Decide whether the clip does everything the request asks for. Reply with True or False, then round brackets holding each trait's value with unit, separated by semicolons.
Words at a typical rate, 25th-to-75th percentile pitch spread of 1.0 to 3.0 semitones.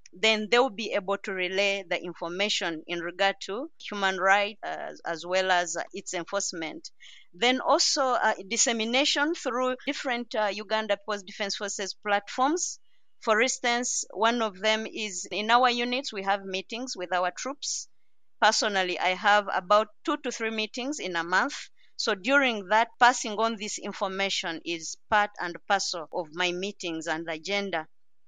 False (160 wpm; 4.3 semitones)